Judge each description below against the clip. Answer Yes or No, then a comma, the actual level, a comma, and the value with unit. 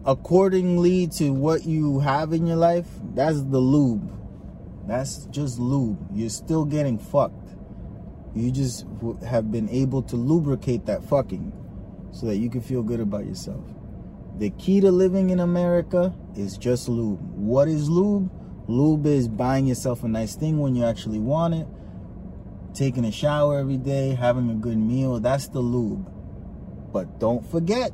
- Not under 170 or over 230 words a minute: No, average, 160 wpm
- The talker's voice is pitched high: No, low, 130 Hz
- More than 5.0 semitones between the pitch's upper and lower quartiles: Yes, wide, 5.6 semitones